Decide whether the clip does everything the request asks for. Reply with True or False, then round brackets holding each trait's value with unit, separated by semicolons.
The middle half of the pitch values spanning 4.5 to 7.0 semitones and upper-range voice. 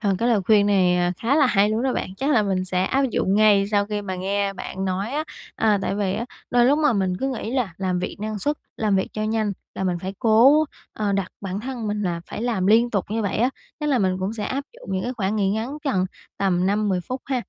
False (3.8 semitones; 210 Hz)